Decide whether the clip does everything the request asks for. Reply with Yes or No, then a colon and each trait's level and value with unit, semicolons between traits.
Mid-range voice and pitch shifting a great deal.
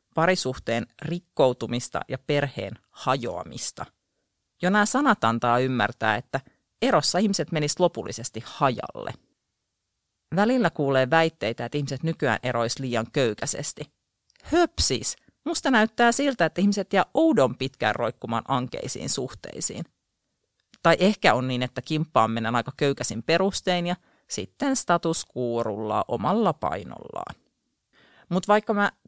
Yes: medium, 150 Hz; wide, 7.9 semitones